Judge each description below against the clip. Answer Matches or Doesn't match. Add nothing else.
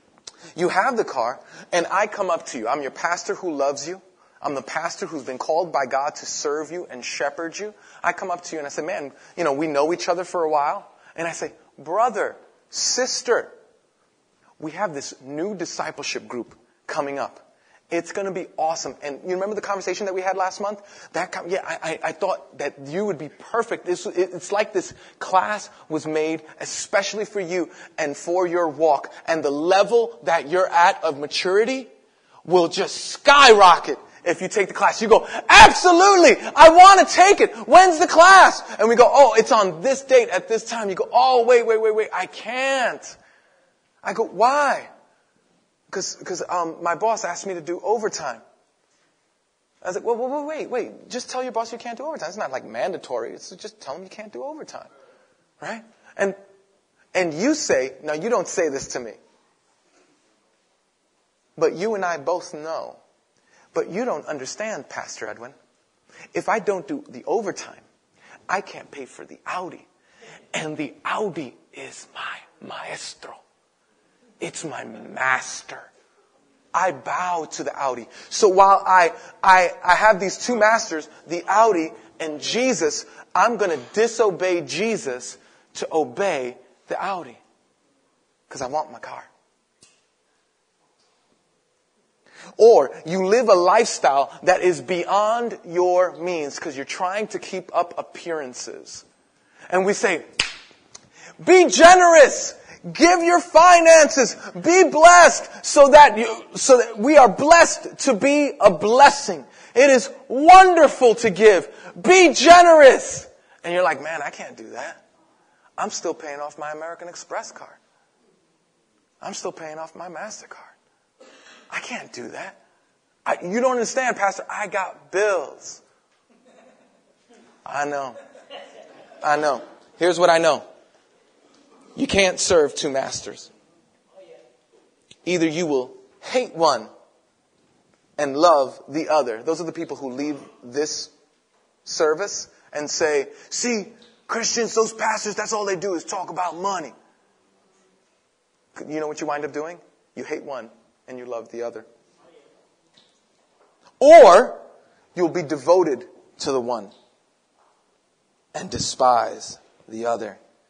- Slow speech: Doesn't match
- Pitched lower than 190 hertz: Doesn't match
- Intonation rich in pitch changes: Matches